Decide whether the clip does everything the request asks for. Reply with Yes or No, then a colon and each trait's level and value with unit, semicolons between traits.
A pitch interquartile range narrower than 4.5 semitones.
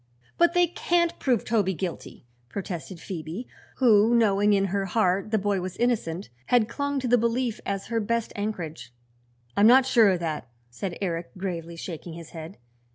No: average, 5.0 semitones